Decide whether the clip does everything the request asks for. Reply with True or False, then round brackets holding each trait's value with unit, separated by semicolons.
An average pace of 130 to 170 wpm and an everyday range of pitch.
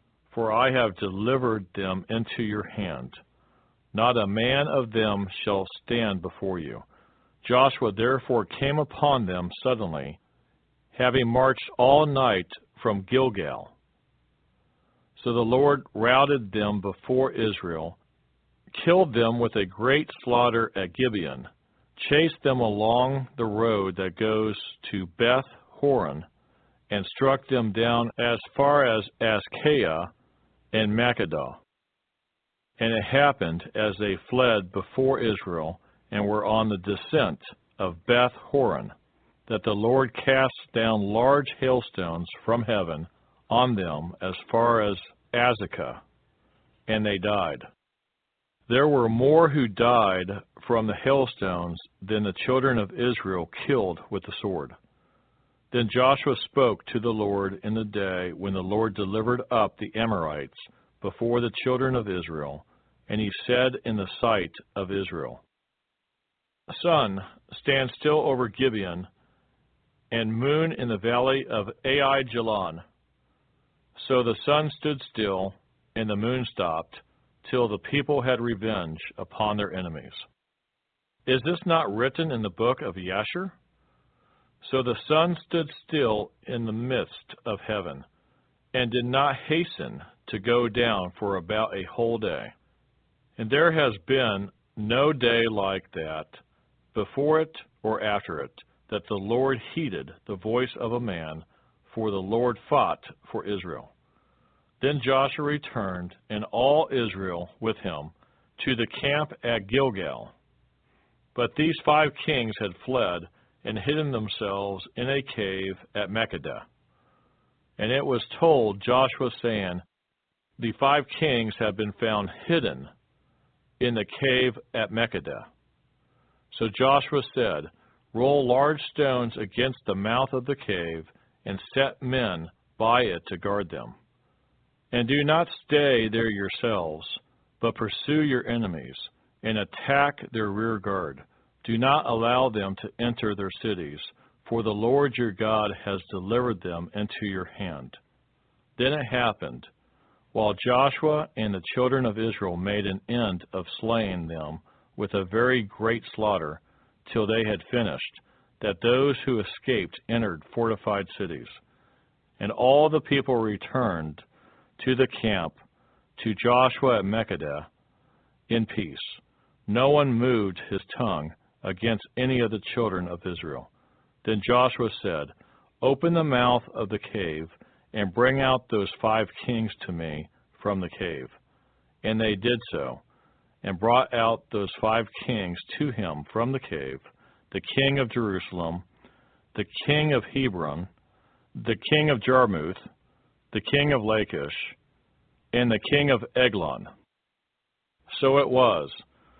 True (135 wpm; 4.5 semitones)